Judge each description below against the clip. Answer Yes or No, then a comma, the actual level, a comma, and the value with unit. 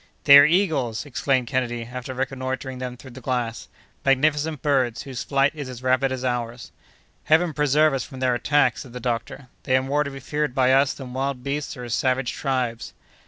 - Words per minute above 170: Yes, average, 195 wpm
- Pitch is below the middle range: Yes, low, 130 Hz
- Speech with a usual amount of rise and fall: No, narrow, 2.1 semitones